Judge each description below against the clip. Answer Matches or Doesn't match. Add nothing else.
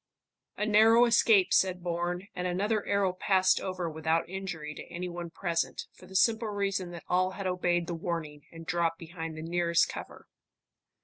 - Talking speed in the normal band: Matches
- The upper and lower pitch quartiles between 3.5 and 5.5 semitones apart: Doesn't match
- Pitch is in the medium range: Matches